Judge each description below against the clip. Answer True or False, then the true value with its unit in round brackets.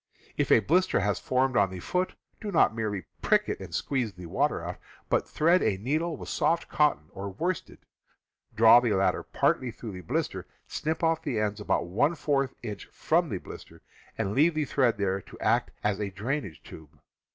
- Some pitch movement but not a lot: False (7.3 semitones)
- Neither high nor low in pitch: False (115 Hz)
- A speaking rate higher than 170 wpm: True (195 wpm)